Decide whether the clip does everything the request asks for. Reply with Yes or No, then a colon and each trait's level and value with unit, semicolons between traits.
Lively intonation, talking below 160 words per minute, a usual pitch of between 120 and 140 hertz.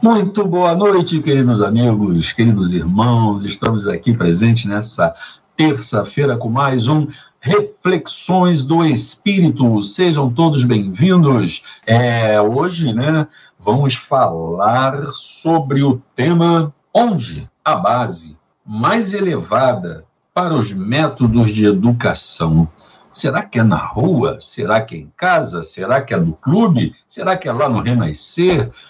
Yes: wide, 7.2 semitones; average, 125 wpm; low, 135 Hz